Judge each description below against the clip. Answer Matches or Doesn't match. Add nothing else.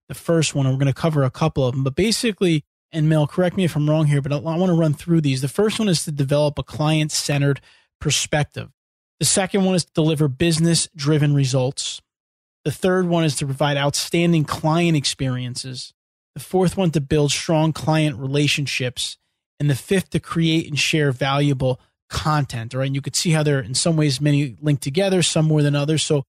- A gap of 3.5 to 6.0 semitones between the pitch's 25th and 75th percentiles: Doesn't match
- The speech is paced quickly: Matches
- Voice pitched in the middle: Matches